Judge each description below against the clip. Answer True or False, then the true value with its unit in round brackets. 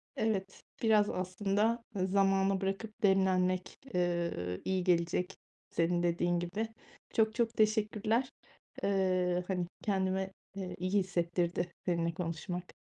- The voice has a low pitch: False (185 Hz)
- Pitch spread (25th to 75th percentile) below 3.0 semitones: True (2.5 semitones)